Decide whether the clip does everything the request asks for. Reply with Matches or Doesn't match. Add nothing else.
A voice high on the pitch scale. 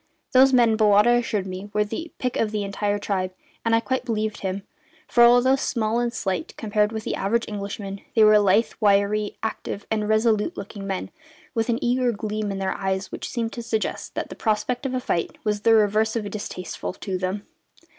Matches